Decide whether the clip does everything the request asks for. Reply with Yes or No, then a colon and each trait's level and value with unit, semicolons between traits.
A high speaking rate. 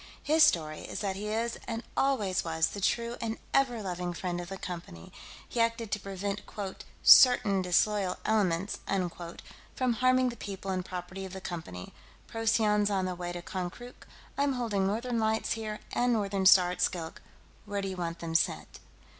No: average, 180 wpm